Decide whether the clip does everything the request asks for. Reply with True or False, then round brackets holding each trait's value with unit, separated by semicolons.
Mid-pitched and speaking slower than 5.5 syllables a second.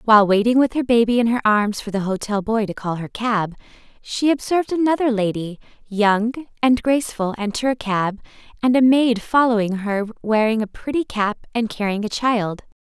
False (225 Hz; 5.2 syllables/s)